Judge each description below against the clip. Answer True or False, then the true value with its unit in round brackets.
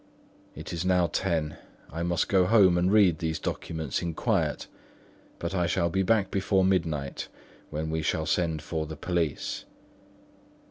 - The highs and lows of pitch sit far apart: False (2.8 semitones)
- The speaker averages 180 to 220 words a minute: False (155 wpm)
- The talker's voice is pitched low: True (85 Hz)